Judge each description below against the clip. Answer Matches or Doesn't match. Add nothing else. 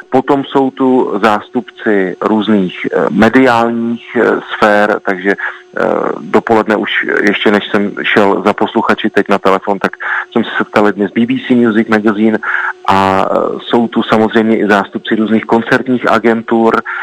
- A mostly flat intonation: Matches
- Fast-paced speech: Doesn't match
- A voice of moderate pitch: Doesn't match